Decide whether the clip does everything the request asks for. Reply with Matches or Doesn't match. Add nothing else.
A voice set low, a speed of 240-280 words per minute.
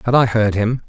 Matches